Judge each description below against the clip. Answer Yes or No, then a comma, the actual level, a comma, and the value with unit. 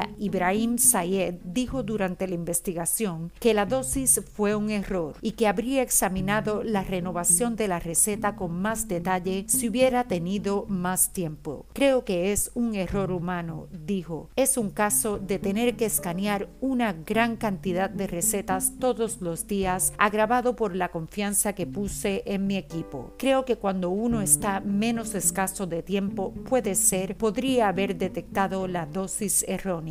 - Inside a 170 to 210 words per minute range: No, average, 155 wpm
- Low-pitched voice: No, high, 200 Hz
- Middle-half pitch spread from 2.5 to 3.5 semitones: Yes, average, 3.2 semitones